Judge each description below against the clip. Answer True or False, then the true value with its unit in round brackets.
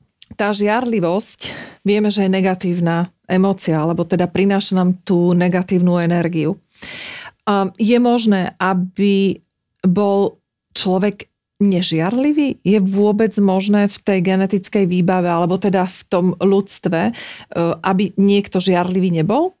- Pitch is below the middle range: False (190 Hz)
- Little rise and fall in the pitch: True (2.1 semitones)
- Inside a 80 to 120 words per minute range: True (115 wpm)